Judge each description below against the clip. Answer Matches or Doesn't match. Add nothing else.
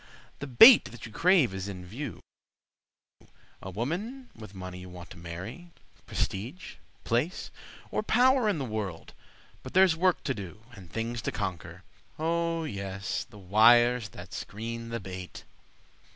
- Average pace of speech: Matches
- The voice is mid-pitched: Doesn't match